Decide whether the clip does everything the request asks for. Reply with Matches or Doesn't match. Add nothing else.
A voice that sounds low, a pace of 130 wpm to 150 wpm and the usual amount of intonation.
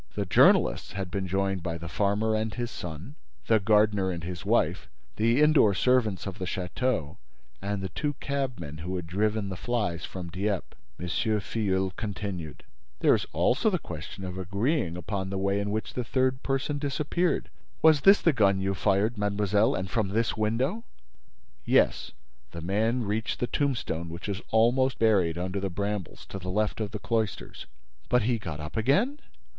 Doesn't match